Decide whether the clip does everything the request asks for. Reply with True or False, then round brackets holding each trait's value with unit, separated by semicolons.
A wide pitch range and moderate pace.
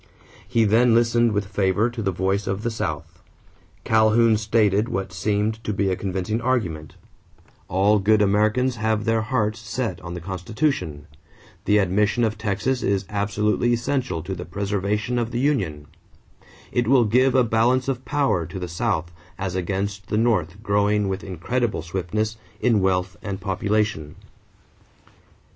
False (3.3 semitones; 155 wpm)